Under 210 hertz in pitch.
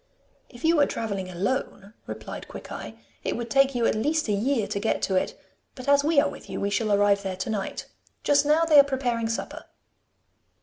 No: high, 235 Hz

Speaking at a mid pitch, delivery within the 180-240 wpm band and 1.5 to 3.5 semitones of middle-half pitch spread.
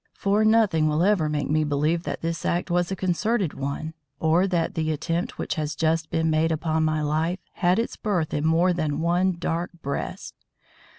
Yes: medium, 165 Hz; average, 190 wpm; narrow, 2.4 semitones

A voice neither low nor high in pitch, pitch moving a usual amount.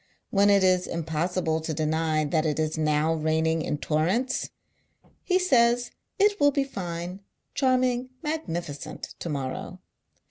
No: medium, 170 Hz; wide, 7.6 semitones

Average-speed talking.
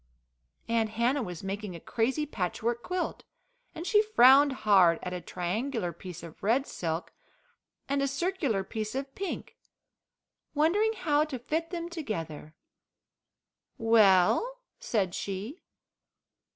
No: slow, 120 wpm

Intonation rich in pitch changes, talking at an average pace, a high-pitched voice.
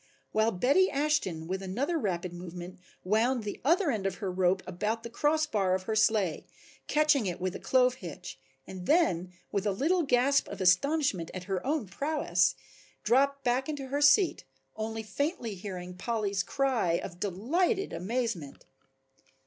Yes: wide, 7.2 semitones; average, 160 wpm; high, 220 Hz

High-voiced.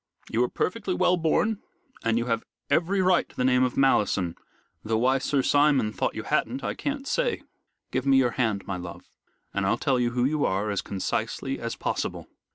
No: low, 130 Hz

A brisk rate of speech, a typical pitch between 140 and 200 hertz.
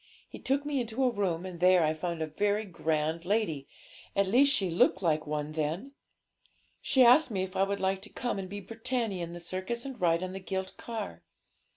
Yes: fast, 215 wpm; high, 190 Hz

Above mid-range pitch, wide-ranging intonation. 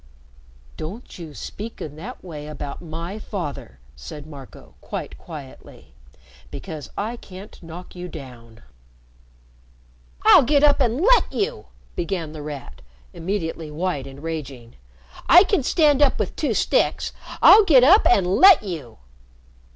No: medium, 170 Hz; wide, 8.5 semitones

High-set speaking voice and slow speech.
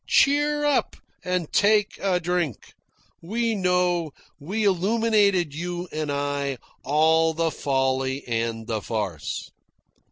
No: medium, 170 Hz; slow, 115 wpm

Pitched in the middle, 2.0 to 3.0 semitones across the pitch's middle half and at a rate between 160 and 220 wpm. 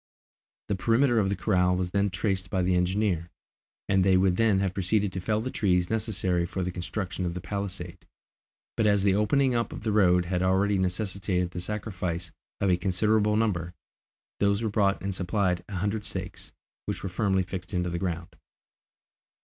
No: very low, 95 Hz; narrow, 2.5 semitones; average, 185 wpm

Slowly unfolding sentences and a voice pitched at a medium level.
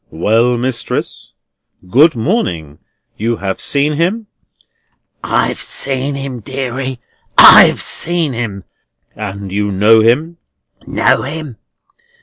No: slow, 105 wpm; low, 125 Hz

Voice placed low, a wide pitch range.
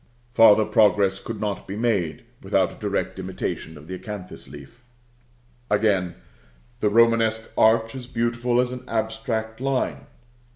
No: low, 110 Hz; narrow, 2.5 semitones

